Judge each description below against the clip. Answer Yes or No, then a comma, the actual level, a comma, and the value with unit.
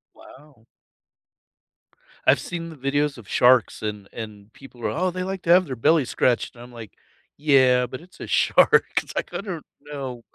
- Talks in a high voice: No, low, 135 Hz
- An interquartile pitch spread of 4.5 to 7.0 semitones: Yes, average, 5.2 semitones